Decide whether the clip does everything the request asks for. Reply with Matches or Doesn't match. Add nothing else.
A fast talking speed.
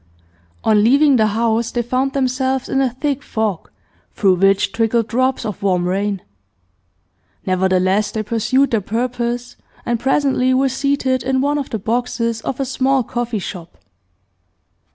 Doesn't match